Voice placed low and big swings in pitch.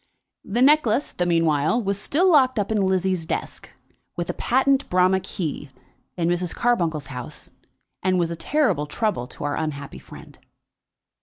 No: medium, 185 Hz; wide, 6.5 semitones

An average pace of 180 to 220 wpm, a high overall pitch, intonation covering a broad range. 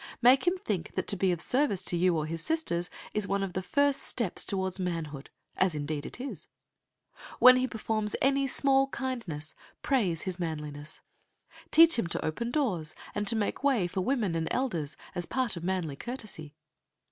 Yes: average, 185 wpm; high, 195 Hz; wide, 7.3 semitones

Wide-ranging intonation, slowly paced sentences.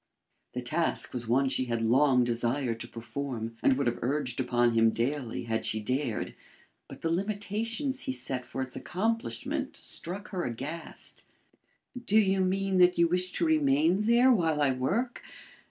No: wide, 7.8 semitones; average, 165 wpm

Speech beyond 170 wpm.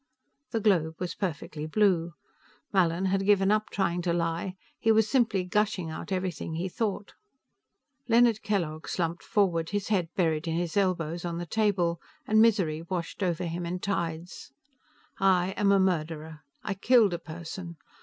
No: average, 160 wpm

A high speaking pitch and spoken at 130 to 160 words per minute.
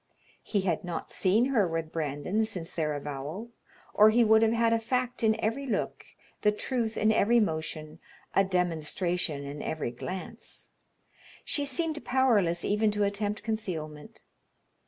Yes: high, 205 Hz; average, 150 wpm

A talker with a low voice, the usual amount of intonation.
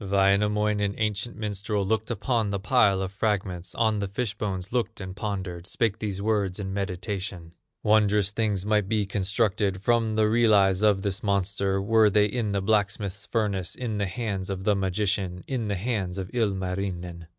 No: low, 100 Hz; narrow, 2.0 semitones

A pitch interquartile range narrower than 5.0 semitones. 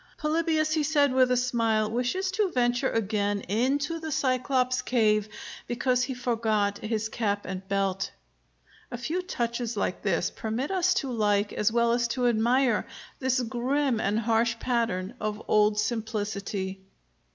Yes: average, 3.5 semitones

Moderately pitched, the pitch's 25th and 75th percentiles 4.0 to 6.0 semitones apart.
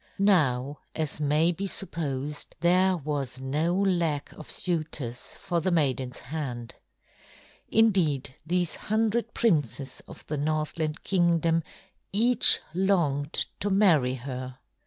Yes: medium, 155 Hz; average, 4.7 semitones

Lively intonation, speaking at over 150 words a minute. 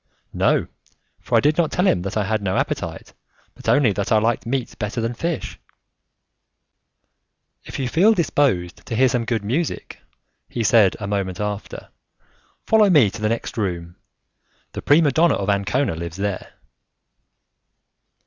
Yes: wide, 6.1 semitones; average, 160 wpm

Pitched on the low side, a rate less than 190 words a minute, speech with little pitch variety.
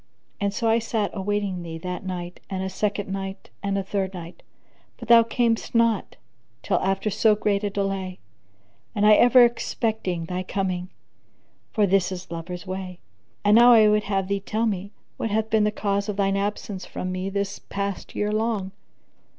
No: high, 200 Hz; average, 175 wpm; narrow, 2.2 semitones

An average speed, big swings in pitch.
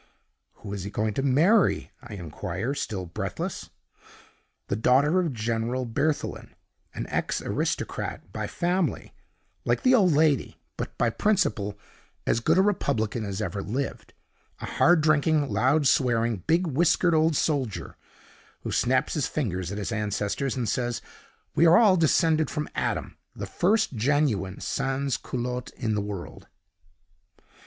Yes: average, 145 wpm; wide, 6.5 semitones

